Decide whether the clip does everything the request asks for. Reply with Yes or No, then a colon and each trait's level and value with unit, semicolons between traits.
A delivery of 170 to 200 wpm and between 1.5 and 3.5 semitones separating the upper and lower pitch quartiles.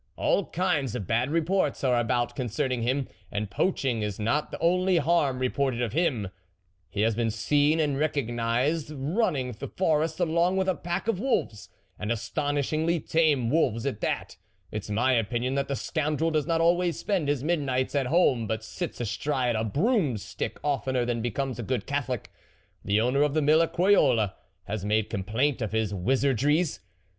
No: average, 175 wpm; average, 5.3 semitones